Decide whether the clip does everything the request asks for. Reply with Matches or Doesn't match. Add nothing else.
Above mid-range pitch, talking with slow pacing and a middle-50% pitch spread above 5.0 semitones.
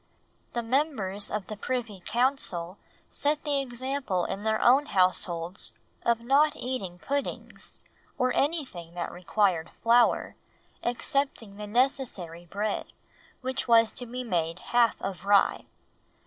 Matches